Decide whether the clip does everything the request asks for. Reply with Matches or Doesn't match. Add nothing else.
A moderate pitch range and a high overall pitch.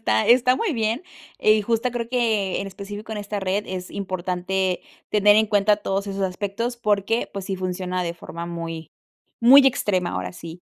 Matches